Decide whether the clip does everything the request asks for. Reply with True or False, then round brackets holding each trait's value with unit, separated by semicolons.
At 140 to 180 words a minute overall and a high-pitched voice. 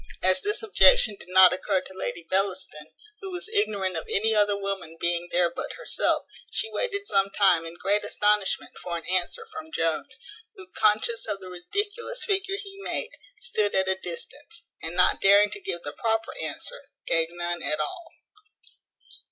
True (175 wpm; 200 Hz)